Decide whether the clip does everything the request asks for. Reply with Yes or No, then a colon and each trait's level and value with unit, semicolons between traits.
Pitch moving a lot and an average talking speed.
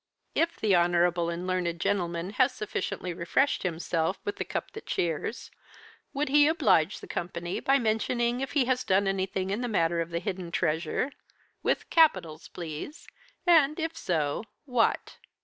Yes: wide, 6.9 semitones; average, 160 wpm